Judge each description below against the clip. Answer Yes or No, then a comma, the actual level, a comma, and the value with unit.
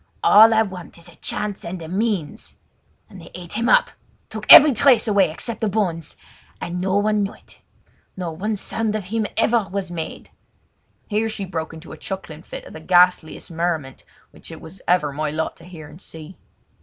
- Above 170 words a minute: Yes, average, 195 wpm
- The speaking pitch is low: No, medium, 185 Hz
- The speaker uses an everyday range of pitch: Yes, average, 4.3 semitones